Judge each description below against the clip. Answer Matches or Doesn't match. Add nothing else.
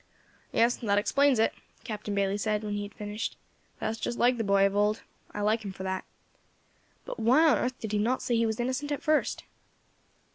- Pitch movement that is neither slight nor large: Matches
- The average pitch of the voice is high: Matches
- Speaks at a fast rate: Matches